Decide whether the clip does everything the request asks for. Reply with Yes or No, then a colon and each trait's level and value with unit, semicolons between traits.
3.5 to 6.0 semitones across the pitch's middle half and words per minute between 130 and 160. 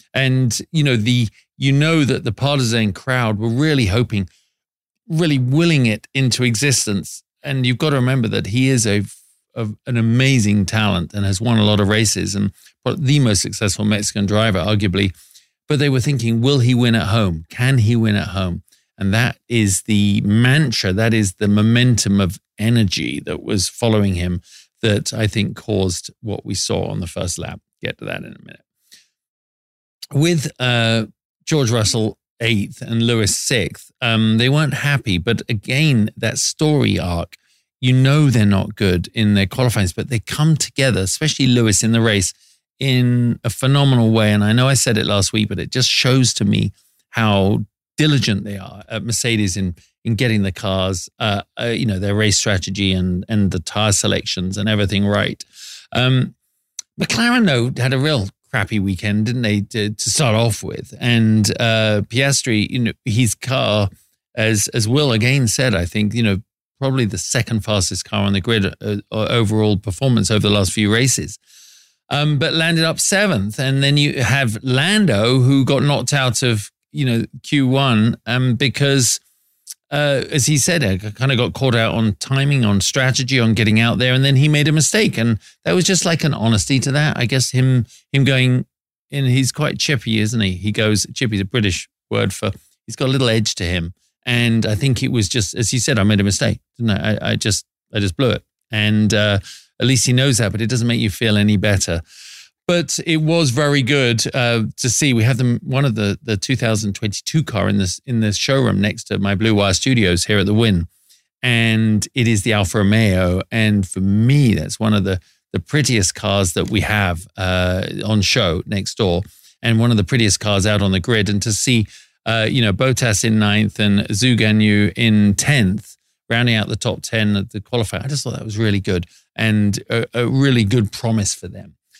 No: average, 3.9 semitones; average, 195 wpm